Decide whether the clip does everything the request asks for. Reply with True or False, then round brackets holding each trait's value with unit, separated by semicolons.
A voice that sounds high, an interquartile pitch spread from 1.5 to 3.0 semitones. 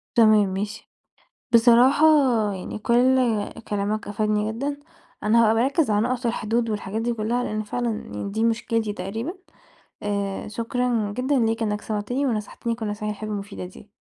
True (220 Hz; 2.4 semitones)